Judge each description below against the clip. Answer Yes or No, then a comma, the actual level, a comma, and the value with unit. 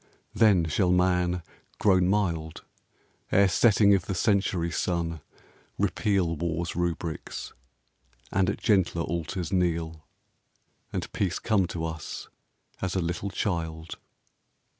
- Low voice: Yes, very low, 90 Hz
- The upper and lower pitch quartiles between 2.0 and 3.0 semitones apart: Yes, average, 2.7 semitones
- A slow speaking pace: Yes, slow, 115 wpm